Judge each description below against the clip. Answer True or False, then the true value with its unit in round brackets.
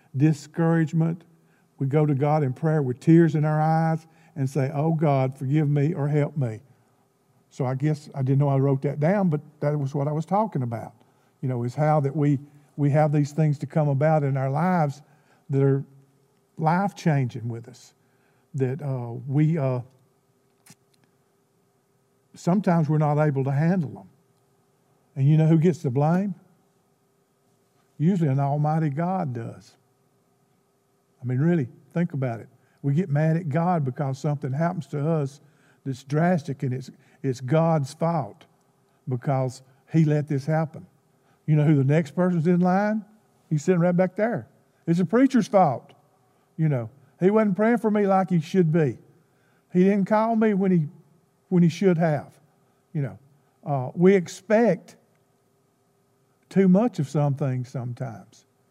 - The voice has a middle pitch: True (145 Hz)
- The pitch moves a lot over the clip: False (3.6 semitones)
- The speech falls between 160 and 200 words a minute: True (165 wpm)